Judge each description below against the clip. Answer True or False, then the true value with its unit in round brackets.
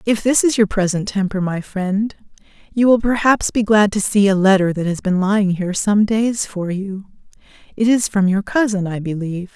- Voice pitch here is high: True (200 Hz)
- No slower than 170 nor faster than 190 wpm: False (205 wpm)